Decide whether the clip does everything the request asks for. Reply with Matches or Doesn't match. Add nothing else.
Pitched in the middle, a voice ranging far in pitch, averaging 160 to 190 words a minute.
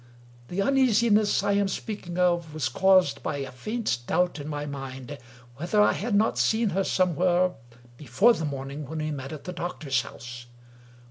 Matches